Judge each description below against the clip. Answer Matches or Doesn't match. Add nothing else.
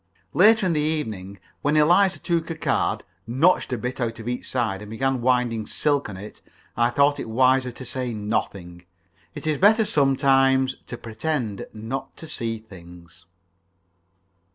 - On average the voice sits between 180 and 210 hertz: Doesn't match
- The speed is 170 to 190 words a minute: Doesn't match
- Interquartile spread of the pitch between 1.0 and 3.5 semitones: Doesn't match